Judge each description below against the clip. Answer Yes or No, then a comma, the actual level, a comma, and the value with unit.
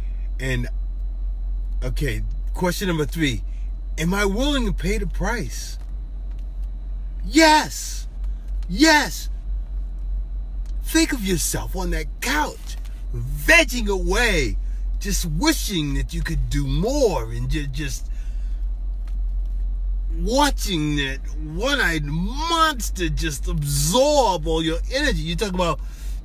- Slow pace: Yes, slow, 100 wpm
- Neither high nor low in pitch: Yes, medium, 155 Hz